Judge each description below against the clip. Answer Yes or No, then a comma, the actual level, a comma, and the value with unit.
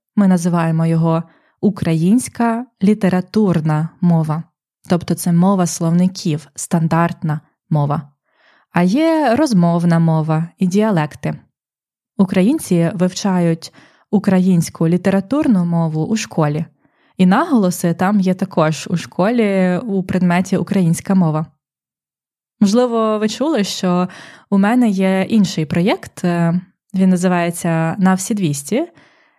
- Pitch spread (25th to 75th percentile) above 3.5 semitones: No, average, 3.2 semitones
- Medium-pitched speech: Yes, medium, 180 Hz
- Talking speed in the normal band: No, slow, 100 wpm